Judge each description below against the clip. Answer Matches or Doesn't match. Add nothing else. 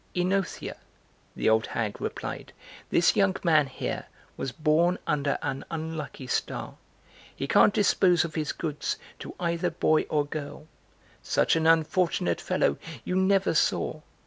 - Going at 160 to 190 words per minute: Doesn't match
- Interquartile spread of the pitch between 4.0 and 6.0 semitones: Doesn't match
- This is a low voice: Doesn't match